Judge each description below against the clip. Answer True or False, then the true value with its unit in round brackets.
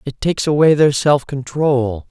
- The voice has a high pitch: False (140 Hz)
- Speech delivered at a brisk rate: False (170 wpm)